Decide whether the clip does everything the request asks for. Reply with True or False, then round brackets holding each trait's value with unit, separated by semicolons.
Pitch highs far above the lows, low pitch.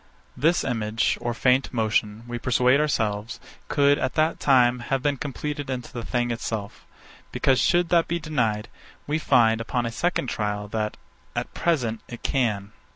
False (4.1 semitones; 125 Hz)